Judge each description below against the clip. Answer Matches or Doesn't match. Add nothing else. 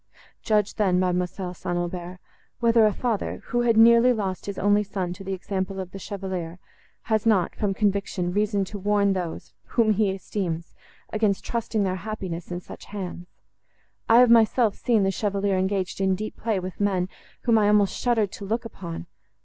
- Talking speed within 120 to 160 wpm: Doesn't match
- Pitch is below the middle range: Doesn't match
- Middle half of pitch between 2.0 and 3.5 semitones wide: Matches